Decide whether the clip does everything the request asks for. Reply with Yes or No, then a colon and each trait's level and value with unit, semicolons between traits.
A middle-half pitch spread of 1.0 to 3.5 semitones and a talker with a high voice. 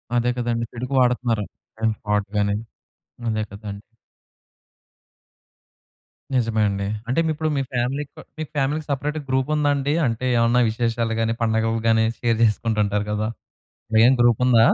No: average, 2.8 semitones; low, 115 Hz